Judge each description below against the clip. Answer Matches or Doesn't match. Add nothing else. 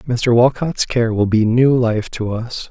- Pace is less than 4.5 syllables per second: Matches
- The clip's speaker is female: Doesn't match